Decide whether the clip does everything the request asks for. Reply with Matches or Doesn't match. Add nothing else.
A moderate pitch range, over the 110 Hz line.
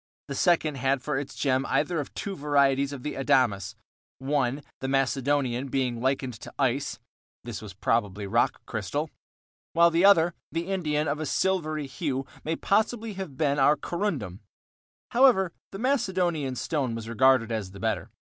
Matches